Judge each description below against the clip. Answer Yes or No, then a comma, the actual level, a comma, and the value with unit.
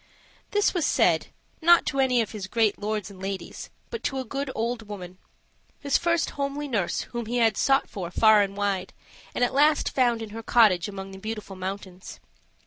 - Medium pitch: No, high, 220 Hz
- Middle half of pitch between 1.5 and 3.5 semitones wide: No, wide, 5.4 semitones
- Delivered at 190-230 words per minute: Yes, average, 195 wpm